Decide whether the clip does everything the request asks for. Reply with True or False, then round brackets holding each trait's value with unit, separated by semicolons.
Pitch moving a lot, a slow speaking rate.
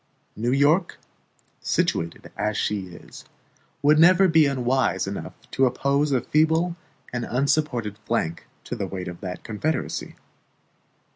True (6.4 semitones; 130 wpm)